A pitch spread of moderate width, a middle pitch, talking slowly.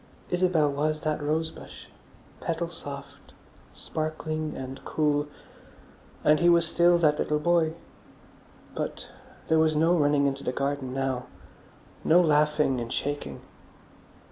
No: narrow, 2.2 semitones; medium, 150 Hz; slow, 125 wpm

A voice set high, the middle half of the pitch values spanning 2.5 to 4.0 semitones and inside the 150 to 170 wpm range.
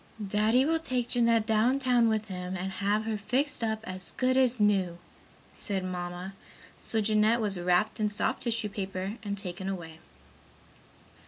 Yes: high, 210 Hz; average, 3.5 semitones; average, 160 wpm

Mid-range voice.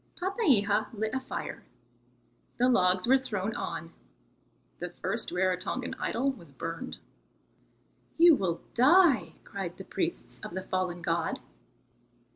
No: high, 200 Hz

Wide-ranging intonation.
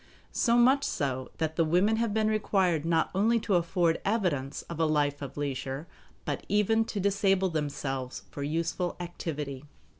Yes: wide, 5.7 semitones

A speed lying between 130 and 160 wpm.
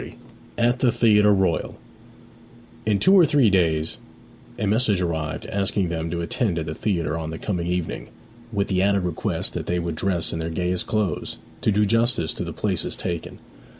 No: average, 185 wpm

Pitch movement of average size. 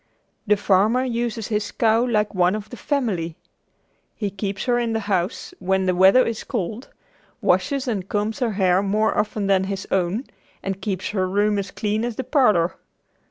Yes: average, 3.1 semitones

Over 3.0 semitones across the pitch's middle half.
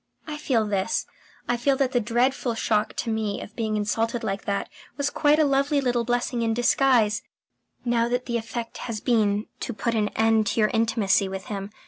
No: average, 2.7 semitones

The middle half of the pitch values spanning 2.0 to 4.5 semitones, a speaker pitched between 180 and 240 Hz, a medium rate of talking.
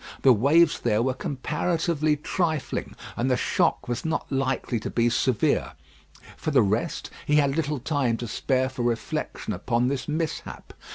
No: average, 4.0 semitones; low, 135 Hz; average, 165 wpm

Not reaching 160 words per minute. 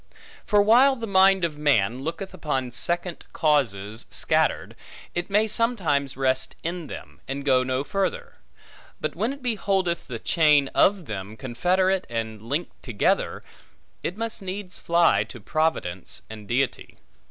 Yes: average, 140 wpm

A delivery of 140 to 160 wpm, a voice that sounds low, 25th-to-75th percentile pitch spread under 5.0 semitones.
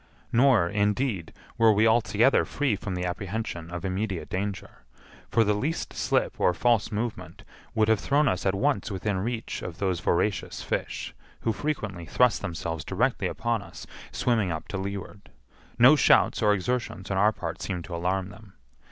No: average, 170 wpm; low, 105 Hz; average, 3.7 semitones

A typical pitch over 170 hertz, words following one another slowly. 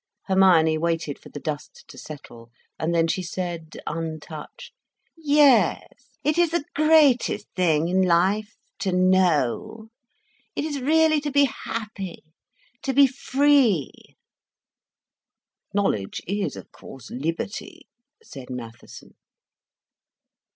Yes: medium, 185 Hz; slow, 110 wpm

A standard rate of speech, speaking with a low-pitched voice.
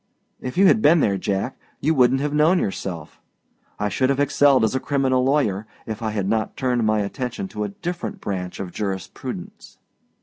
Yes: average, 190 wpm; low, 125 Hz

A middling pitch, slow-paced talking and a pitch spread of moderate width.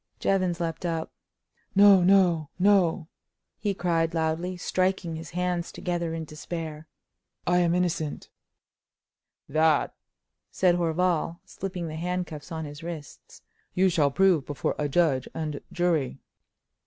No: medium, 170 Hz; slow, 125 wpm; narrow, 2.2 semitones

